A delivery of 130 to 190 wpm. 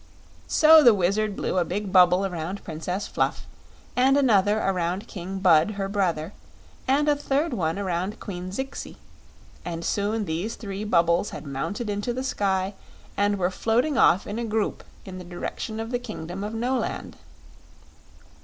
Yes: average, 160 wpm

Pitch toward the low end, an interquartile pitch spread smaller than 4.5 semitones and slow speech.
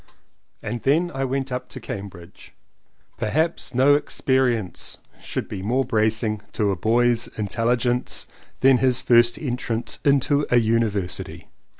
Yes: low, 120 Hz; average, 3.3 semitones; slow, 130 wpm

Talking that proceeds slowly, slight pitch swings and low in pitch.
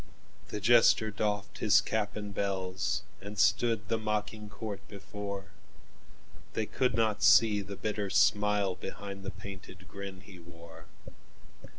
Yes: slow, 115 wpm; narrow, 1.7 semitones; low, 100 Hz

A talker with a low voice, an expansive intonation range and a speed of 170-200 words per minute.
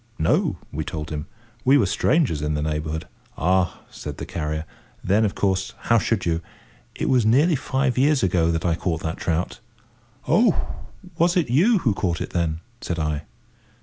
Yes: very low, 90 Hz; wide, 7.5 semitones; average, 180 wpm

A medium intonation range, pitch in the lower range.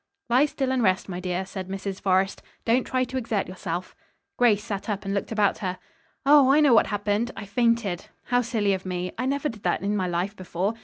No: average, 4.2 semitones; high, 205 Hz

